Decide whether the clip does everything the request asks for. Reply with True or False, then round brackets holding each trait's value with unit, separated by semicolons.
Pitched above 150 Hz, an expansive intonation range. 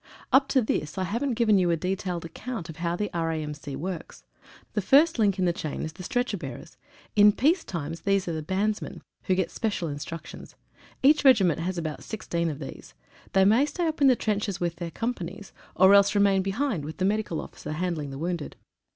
False (190 Hz; 4.5 semitones)